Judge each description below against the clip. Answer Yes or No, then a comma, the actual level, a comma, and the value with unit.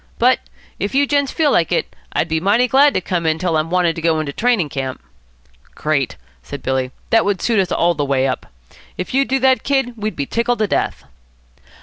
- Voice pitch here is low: No, medium, 185 Hz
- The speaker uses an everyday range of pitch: No, wide, 7.7 semitones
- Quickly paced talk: Yes, fast, 220 wpm